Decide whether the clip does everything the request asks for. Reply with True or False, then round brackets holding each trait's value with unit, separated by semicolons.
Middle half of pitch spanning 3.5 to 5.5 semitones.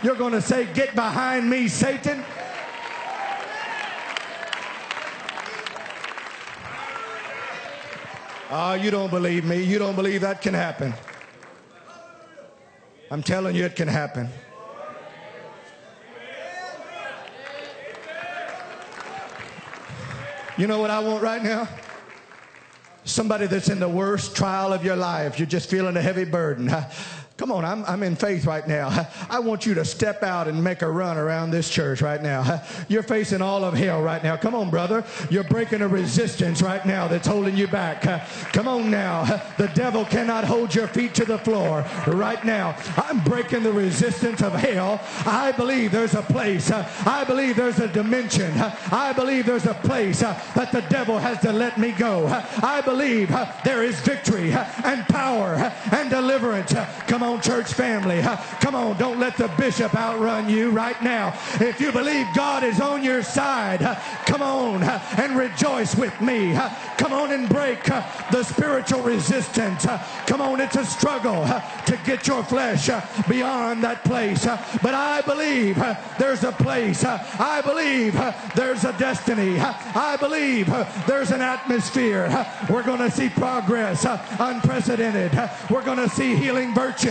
True (5.0 semitones)